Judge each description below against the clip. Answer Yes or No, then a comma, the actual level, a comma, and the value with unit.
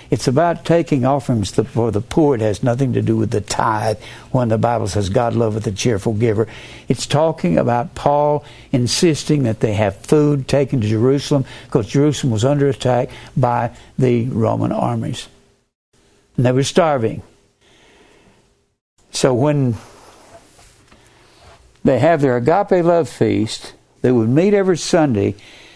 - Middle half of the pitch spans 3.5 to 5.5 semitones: Yes, average, 4.1 semitones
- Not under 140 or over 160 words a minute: Yes, average, 145 wpm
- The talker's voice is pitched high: No, low, 125 Hz